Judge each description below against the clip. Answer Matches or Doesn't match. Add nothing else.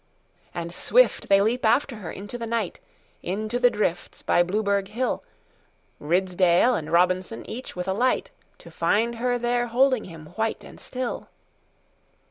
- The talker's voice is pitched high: Matches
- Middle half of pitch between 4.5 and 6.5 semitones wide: Matches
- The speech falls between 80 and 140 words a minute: Matches